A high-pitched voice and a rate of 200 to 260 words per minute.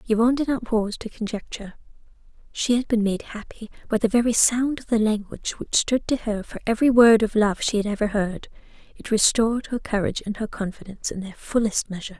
Yes: high, 220 Hz; fast, 205 wpm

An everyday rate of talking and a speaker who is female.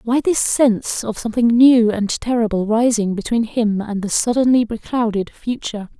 Yes: average, 160 wpm; female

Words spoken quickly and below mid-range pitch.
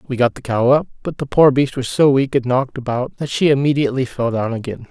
Yes: fast, 255 wpm; low, 130 Hz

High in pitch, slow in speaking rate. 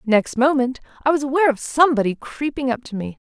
No: very high, 260 Hz; average, 200 wpm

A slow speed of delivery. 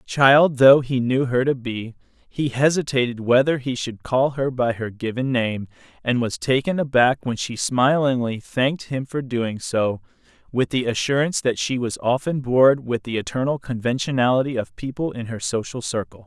No: average, 175 wpm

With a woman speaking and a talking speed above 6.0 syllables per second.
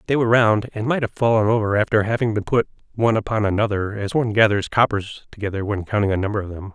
No: male; 6.8 syllables/s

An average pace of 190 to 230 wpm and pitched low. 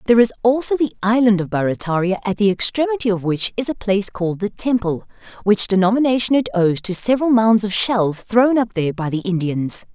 No: average, 200 wpm; high, 210 Hz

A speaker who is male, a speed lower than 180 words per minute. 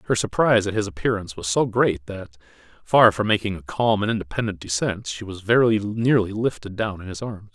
No: male; fast, 205 wpm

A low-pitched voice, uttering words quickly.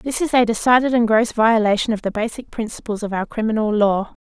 No: high, 225 Hz; fast, 215 wpm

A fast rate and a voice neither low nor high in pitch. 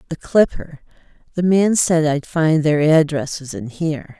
No: average, 155 wpm; medium, 160 Hz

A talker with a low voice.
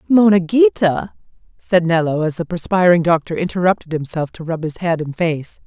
No: medium, 175 Hz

